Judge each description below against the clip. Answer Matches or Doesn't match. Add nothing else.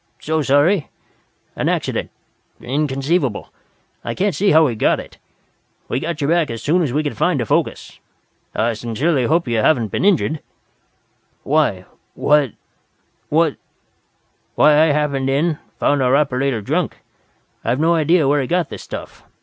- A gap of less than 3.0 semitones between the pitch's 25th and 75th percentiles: Doesn't match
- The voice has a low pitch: Doesn't match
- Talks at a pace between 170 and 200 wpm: Doesn't match